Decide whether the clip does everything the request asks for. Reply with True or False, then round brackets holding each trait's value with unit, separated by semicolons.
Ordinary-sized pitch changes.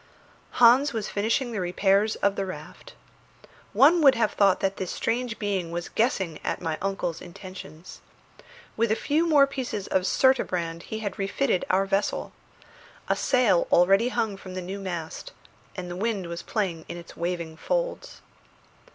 True (4.5 semitones)